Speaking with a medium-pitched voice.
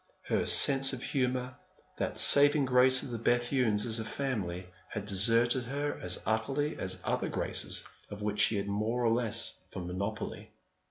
No: low, 115 Hz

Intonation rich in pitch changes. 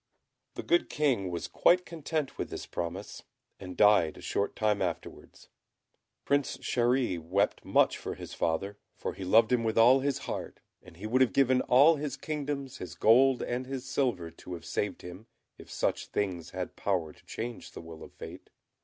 Yes: wide, 6.6 semitones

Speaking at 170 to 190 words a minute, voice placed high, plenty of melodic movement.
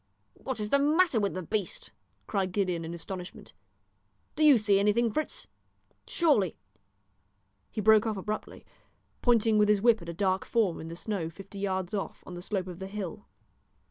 No: average, 180 wpm; high, 200 Hz; average, 3.5 semitones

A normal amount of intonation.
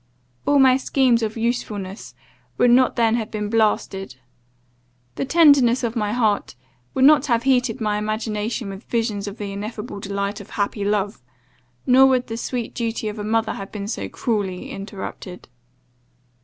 Yes: average, 3.1 semitones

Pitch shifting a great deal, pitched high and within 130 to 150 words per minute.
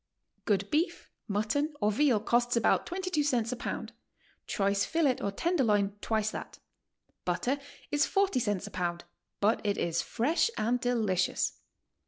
Yes: wide, 6.1 semitones; high, 230 Hz; average, 145 wpm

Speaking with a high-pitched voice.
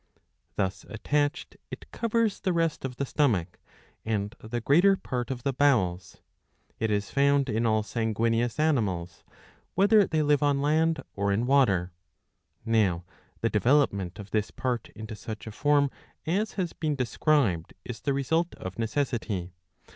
No: low, 120 Hz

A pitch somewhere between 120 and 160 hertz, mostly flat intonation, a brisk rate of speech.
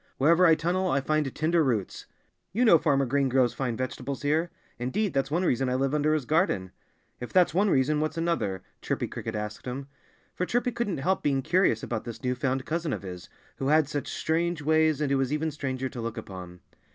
No: medium, 140 Hz; average, 4.3 semitones; fast, 215 wpm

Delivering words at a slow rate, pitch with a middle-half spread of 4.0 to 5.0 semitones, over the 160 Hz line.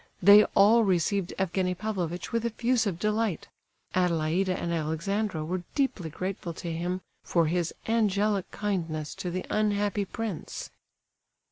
No: slow, 125 wpm; average, 3.6 semitones; high, 190 Hz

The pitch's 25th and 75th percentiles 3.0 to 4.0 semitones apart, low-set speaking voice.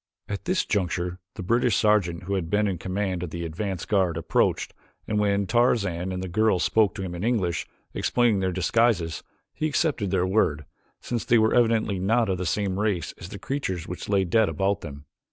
Yes: average, 3.5 semitones; low, 100 Hz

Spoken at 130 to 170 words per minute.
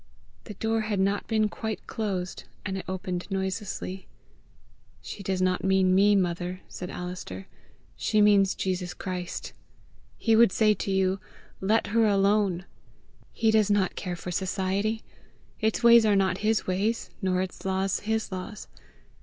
Yes: average, 150 wpm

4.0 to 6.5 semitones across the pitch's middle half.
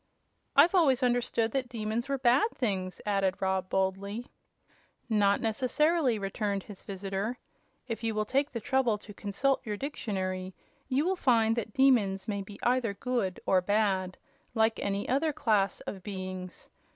Yes: average, 4.3 semitones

